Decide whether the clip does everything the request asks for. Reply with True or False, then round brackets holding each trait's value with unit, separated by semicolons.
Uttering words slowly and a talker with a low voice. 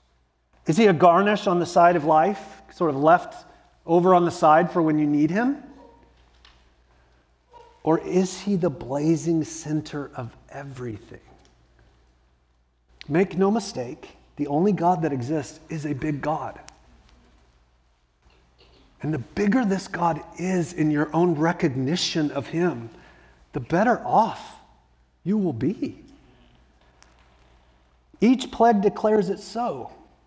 False (125 wpm; 155 Hz)